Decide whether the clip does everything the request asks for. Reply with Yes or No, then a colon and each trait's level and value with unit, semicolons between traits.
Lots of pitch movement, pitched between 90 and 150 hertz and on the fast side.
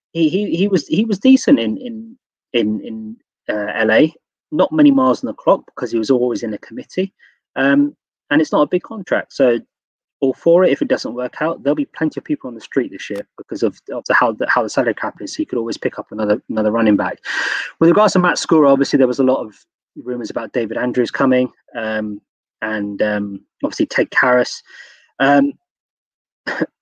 Yes: wide, 7.8 semitones; medium, 140 Hz; fast, 215 wpm